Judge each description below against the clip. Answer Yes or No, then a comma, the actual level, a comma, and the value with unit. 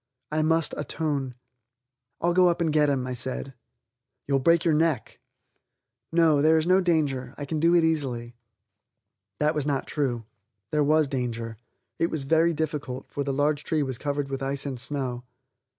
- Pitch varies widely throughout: No, average, 3.0 semitones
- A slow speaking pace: No, average, 175 wpm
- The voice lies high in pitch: No, medium, 145 Hz